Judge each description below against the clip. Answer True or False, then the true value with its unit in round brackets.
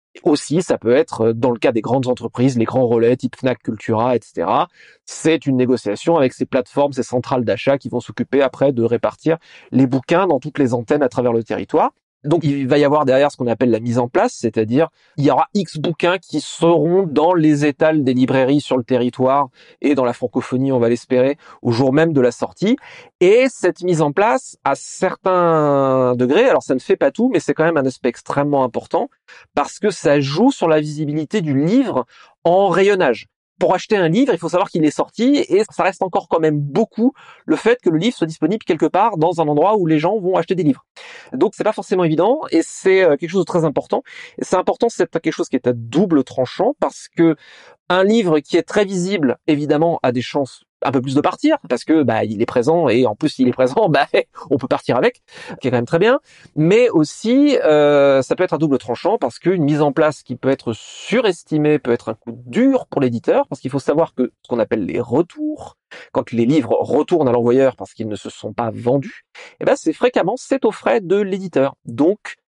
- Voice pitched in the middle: True (150 Hz)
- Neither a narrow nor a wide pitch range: False (6.3 semitones)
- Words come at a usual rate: False (230 wpm)